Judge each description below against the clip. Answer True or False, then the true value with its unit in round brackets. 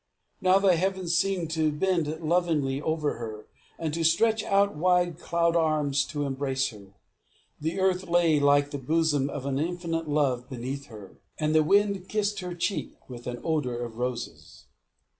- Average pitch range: True (4.3 semitones)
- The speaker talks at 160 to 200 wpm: True (165 wpm)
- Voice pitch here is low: False (155 Hz)